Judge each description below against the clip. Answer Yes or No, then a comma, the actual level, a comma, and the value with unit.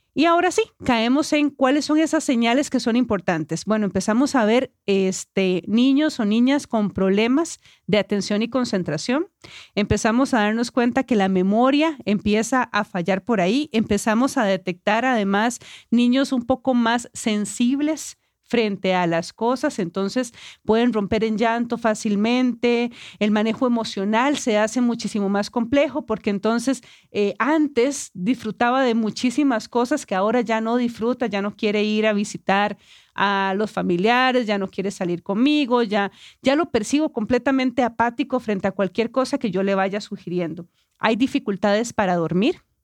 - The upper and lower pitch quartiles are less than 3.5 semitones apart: No, average, 3.9 semitones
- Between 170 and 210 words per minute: No, average, 155 wpm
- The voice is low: No, high, 230 Hz